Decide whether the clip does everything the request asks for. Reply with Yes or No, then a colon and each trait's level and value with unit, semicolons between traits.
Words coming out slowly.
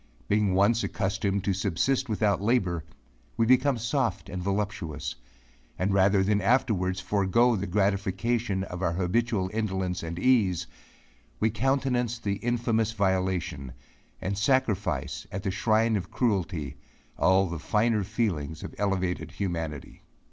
Yes: slow, 130 wpm